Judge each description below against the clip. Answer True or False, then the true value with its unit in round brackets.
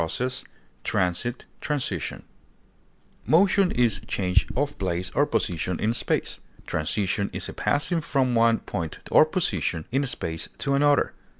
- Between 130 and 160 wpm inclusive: True (135 wpm)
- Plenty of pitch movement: True (7.9 semitones)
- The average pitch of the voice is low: True (115 Hz)